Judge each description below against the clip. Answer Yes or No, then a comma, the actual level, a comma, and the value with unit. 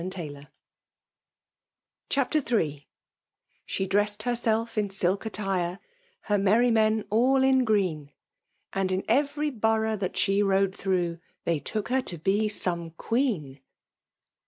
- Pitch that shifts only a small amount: No, average, 3.8 semitones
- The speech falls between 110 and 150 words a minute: Yes, slow, 135 wpm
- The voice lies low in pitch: No, high, 205 Hz